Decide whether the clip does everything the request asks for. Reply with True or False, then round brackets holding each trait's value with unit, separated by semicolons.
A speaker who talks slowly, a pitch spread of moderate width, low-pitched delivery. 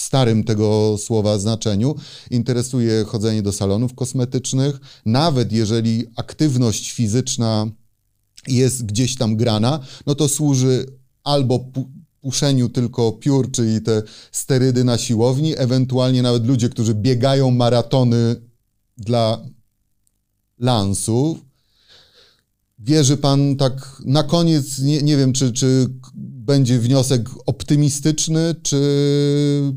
True (105 wpm; 3.2 semitones; 125 Hz)